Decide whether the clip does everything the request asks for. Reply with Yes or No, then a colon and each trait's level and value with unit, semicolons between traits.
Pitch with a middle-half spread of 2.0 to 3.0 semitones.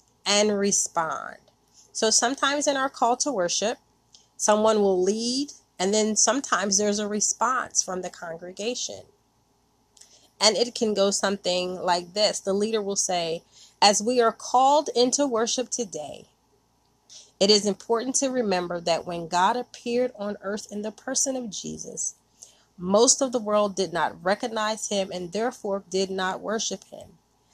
No: average, 4.0 semitones